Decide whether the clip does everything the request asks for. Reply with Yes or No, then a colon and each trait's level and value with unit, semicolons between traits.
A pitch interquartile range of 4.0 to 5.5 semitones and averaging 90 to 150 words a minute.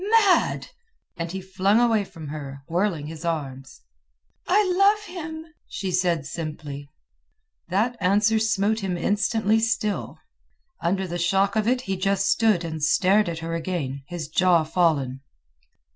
Yes: average, 4.8 semitones; average, 145 wpm